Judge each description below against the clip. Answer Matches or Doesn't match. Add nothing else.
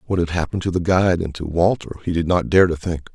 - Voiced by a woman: Doesn't match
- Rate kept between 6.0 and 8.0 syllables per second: Matches